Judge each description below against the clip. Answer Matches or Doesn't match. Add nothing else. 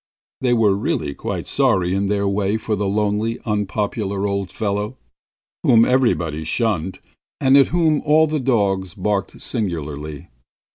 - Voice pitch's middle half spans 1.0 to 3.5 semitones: Matches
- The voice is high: Doesn't match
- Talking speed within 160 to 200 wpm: Doesn't match